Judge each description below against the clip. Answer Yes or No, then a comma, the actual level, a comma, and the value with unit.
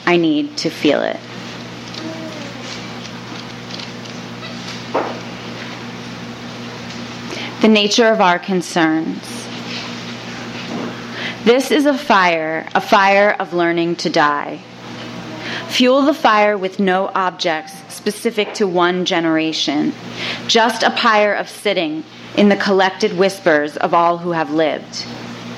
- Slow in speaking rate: Yes, slow, 105 wpm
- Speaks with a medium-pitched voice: Yes, medium, 160 Hz